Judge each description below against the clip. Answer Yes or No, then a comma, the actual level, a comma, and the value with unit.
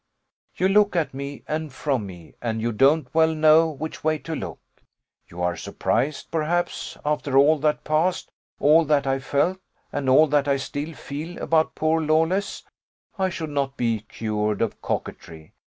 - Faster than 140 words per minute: Yes, average, 170 wpm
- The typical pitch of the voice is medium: Yes, medium, 150 Hz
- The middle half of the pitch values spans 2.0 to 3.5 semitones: Yes, average, 3.2 semitones